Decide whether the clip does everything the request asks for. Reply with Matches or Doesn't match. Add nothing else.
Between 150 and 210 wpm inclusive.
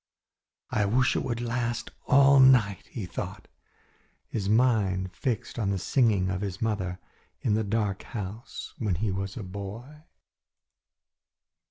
Doesn't match